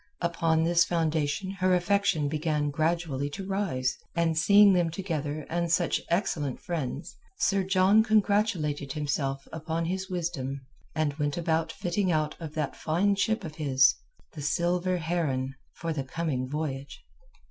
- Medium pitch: Yes, medium, 165 Hz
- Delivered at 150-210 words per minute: No, average, 140 wpm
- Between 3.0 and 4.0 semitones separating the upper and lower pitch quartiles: Yes, average, 3.6 semitones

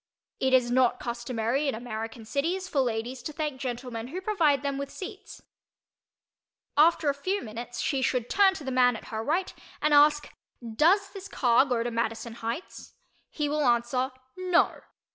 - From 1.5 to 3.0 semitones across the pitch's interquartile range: No, average, 4.3 semitones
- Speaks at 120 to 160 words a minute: No, average, 170 wpm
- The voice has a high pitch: Yes, very high, 265 Hz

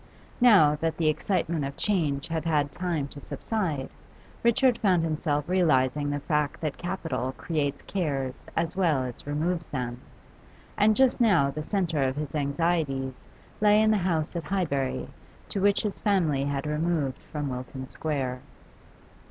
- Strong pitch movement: No, average, 4.4 semitones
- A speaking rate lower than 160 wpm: Yes, average, 150 wpm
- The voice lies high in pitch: No, medium, 155 Hz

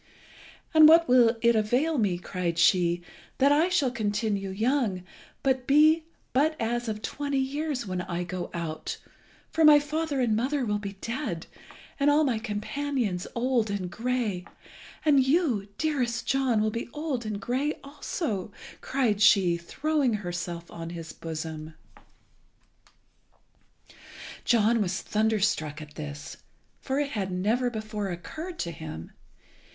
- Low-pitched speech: No, high, 225 Hz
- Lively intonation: Yes, wide, 7.0 semitones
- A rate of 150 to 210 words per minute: No, average, 140 wpm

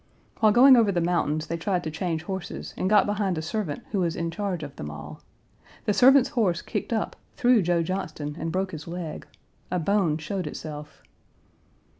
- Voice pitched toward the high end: No, medium, 175 Hz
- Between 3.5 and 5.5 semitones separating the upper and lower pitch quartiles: Yes, average, 4.4 semitones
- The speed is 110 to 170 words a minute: No, average, 190 wpm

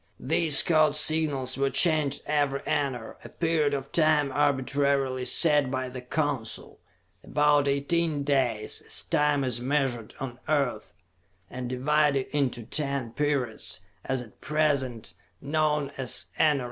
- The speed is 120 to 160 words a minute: Yes, slow, 135 wpm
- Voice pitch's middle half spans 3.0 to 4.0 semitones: No, narrow, 2.5 semitones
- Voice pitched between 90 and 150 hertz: Yes, medium, 140 Hz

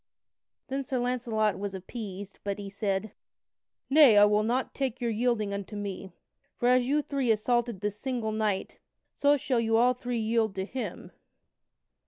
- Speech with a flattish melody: No, average, 3.5 semitones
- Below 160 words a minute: No, average, 165 wpm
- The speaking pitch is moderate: No, high, 225 Hz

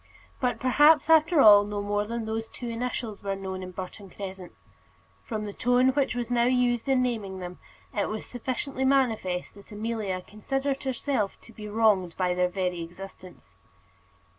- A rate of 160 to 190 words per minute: Yes, average, 165 wpm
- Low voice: No, high, 220 Hz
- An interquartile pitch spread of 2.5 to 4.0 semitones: No, average, 4.4 semitones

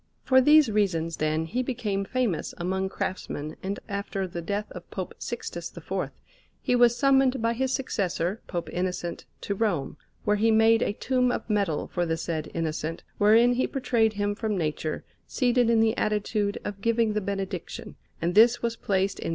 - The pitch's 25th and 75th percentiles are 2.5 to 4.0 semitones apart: No, average, 4.4 semitones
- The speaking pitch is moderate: No, high, 205 Hz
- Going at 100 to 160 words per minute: No, average, 180 wpm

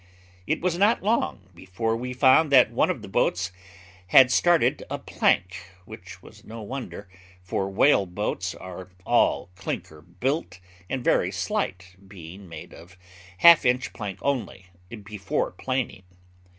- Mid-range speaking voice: No, low, 100 Hz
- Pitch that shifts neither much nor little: No, wide, 6.1 semitones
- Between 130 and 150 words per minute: Yes, average, 140 wpm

